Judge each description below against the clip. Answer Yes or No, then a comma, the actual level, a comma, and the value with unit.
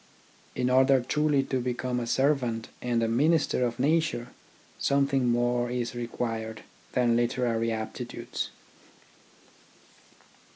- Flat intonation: Yes, narrow, 2.3 semitones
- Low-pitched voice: Yes, low, 125 Hz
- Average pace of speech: No, slow, 110 wpm